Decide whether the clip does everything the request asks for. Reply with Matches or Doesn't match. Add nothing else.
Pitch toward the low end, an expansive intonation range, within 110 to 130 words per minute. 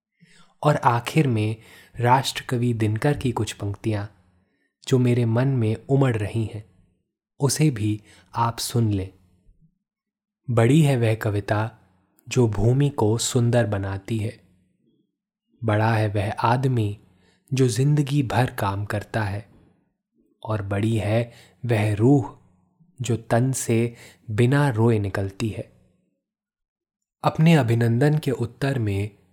Doesn't match